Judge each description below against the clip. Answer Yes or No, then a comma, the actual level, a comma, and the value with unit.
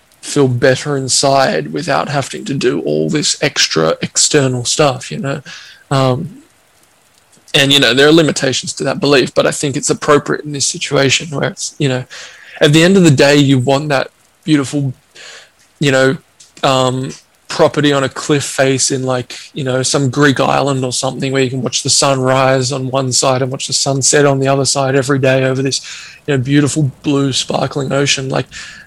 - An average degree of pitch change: No, narrow, 1.7 semitones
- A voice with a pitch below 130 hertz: No, low, 135 Hz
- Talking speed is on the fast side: No, average, 195 wpm